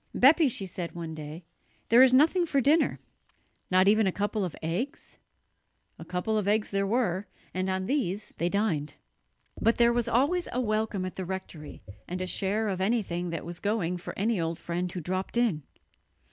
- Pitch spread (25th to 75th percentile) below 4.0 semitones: No, average, 4.6 semitones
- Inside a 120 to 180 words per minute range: No, average, 190 wpm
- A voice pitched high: Yes, high, 195 Hz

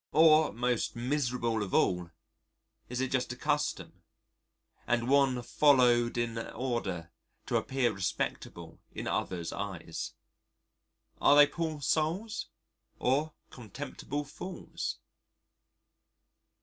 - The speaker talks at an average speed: No, slow, 100 wpm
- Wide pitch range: No, average, 4.0 semitones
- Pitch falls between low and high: No, low, 125 Hz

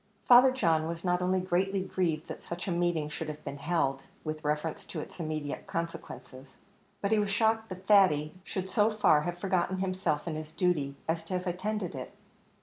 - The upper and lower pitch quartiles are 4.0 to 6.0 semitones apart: No, average, 3.6 semitones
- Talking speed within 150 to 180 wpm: No, average, 195 wpm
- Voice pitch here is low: No, medium, 175 Hz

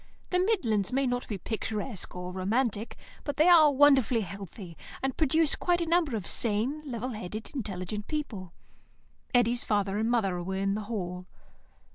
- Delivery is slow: No, average, 160 wpm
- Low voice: No, high, 225 Hz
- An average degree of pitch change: No, wide, 5.7 semitones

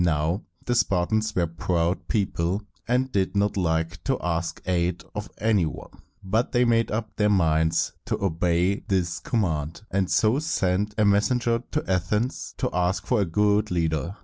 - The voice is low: Yes, very low, 95 Hz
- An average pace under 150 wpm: No, average, 170 wpm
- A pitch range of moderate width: Yes, average, 3.9 semitones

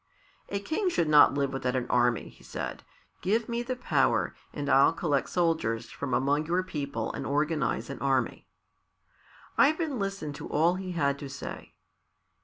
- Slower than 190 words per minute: Yes, average, 165 wpm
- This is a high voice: No, medium, 150 Hz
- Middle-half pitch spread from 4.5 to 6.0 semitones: Yes, average, 5.2 semitones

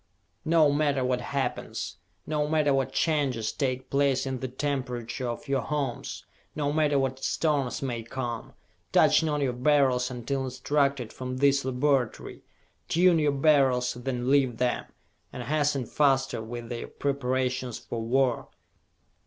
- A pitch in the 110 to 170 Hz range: Yes, low, 135 Hz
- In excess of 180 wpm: No, average, 140 wpm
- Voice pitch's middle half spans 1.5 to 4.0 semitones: Yes, narrow, 2.4 semitones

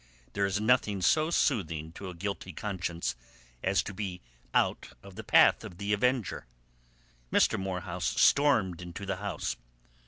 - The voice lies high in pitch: No, low, 100 Hz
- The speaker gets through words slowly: No, average, 150 wpm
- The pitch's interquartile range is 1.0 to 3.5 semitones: Yes, average, 2.7 semitones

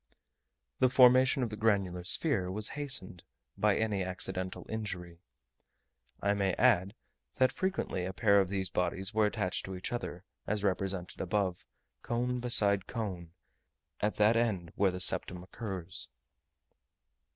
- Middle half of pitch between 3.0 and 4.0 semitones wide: Yes, average, 3.6 semitones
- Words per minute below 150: Yes, average, 140 wpm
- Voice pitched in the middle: No, low, 100 Hz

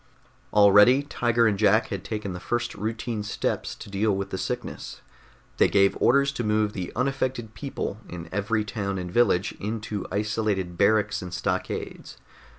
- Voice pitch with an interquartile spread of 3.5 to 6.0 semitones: No, average, 3.0 semitones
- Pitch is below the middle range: Yes, low, 105 Hz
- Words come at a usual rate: Yes, average, 155 wpm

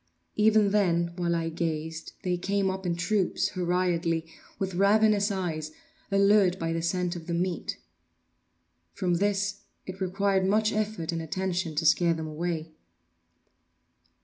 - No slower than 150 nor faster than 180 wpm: No, average, 140 wpm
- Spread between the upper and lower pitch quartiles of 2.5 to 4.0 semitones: Yes, average, 2.9 semitones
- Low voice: No, medium, 180 Hz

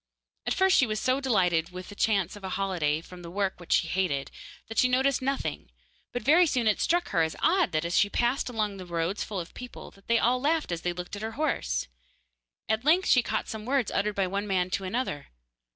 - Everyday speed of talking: No, fast, 230 wpm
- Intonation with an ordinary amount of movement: No, wide, 5.9 semitones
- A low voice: No, high, 205 Hz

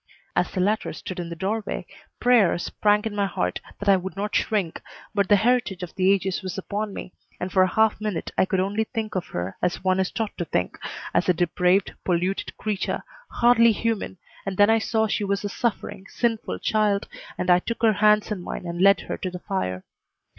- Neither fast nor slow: No, fast, 215 wpm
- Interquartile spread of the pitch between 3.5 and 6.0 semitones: No, average, 2.9 semitones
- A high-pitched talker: Yes, high, 200 Hz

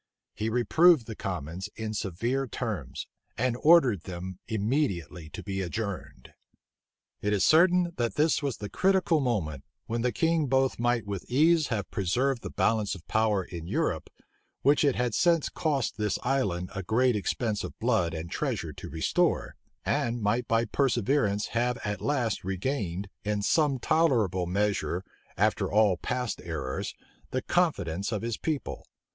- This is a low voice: Yes, low, 110 Hz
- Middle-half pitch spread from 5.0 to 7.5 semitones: Yes, wide, 5.6 semitones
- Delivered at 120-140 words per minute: No, average, 155 wpm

